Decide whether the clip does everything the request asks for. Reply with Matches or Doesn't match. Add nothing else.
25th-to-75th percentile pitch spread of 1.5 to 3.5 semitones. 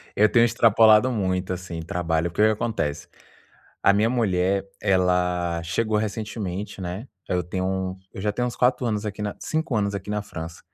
Matches